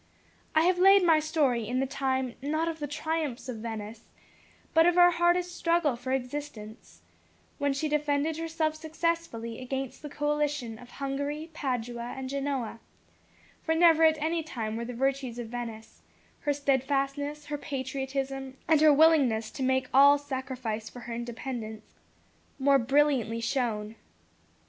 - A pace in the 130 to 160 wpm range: Yes, average, 150 wpm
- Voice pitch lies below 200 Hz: No, very high, 275 Hz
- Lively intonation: No, average, 4.0 semitones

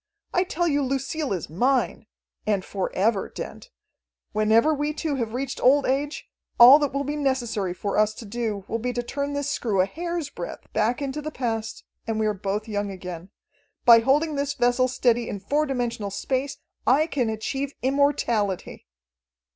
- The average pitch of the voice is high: Yes, high, 245 Hz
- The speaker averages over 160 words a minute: Yes, average, 180 wpm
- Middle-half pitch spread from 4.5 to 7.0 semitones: Yes, average, 4.8 semitones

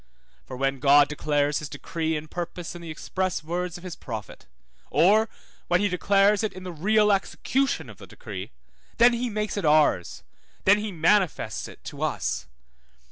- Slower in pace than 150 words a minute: No, average, 175 wpm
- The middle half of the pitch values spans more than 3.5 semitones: Yes, average, 5.1 semitones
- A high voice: No, medium, 180 Hz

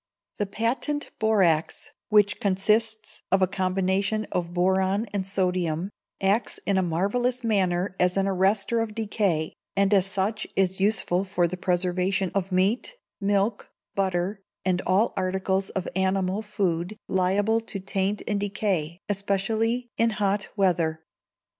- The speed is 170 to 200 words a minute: No, slow, 135 wpm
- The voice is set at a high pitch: Yes, high, 195 Hz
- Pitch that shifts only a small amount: Yes, narrow, 2.2 semitones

